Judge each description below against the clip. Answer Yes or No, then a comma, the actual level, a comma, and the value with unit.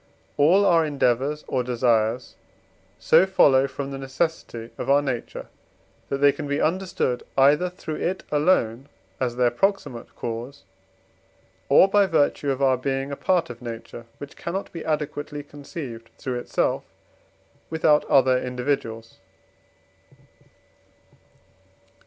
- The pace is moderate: No, slow, 125 wpm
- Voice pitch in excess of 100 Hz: Yes, medium, 140 Hz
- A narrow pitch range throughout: No, average, 3.9 semitones